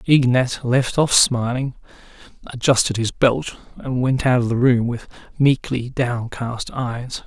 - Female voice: No, male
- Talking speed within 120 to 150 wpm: Yes, average, 140 wpm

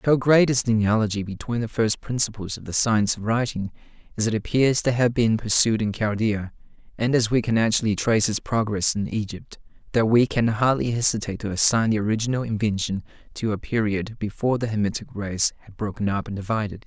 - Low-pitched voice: Yes, low, 110 Hz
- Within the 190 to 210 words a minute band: Yes, average, 195 wpm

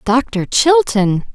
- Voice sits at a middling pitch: No, high, 245 Hz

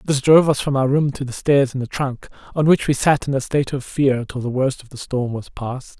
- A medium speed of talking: No, fast, 290 wpm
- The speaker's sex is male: Yes, male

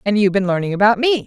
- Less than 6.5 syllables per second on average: No, 7.7 syllables/s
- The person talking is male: No, female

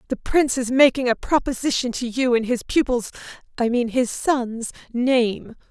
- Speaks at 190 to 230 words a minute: No, average, 145 wpm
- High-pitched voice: Yes, very high, 250 Hz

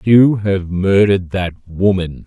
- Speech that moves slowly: Yes, slow, 130 wpm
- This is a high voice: No, very low, 95 Hz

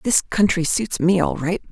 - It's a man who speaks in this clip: No, female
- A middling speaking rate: No, fast, 210 wpm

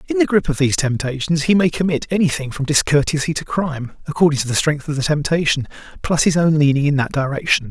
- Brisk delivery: Yes, fast, 210 wpm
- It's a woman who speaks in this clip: No, male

